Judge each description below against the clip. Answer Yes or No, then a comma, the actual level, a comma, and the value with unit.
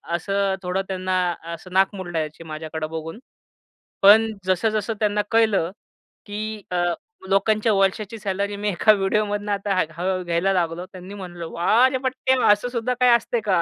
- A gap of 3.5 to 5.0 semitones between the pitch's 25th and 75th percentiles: No, average, 3.0 semitones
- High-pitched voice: Yes, high, 195 Hz